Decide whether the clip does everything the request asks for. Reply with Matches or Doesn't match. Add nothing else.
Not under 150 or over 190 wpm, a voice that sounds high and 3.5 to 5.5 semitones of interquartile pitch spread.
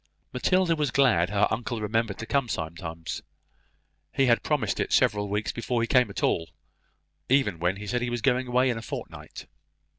Doesn't match